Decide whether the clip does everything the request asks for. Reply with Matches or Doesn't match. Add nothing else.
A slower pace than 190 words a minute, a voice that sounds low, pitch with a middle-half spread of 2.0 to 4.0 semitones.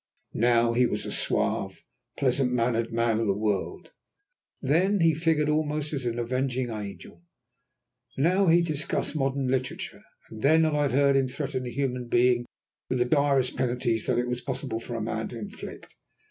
Matches